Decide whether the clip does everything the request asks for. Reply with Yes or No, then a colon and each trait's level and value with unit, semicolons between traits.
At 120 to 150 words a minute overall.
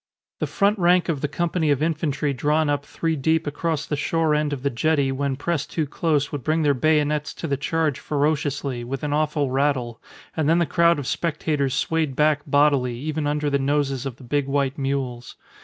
No: fast, 205 wpm